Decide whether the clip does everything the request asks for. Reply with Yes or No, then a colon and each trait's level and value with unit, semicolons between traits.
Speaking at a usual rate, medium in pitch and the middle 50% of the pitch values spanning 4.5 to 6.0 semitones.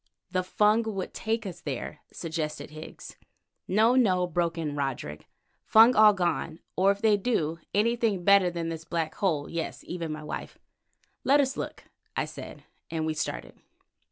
Yes: average, 160 wpm; medium, 175 Hz; average, 4.8 semitones